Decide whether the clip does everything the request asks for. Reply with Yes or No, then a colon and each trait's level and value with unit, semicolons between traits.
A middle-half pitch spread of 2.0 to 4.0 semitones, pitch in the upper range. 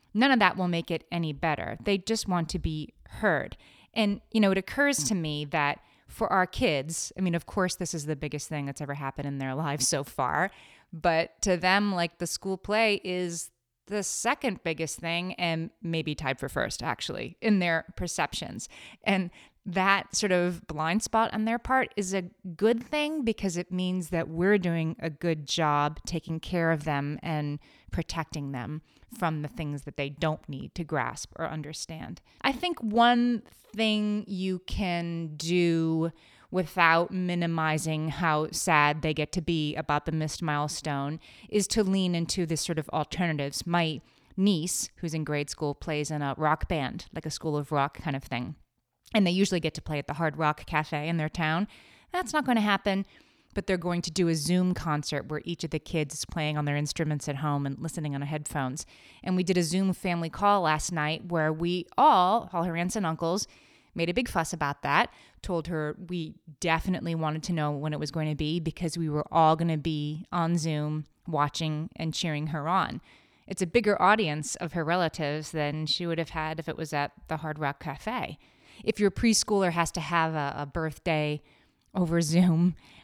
No: average, 3.3 semitones; medium, 165 Hz